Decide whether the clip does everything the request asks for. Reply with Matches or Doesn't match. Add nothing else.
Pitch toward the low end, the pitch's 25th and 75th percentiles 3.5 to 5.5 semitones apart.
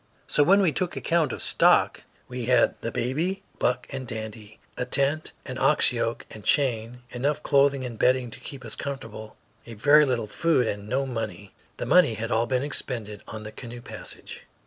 Matches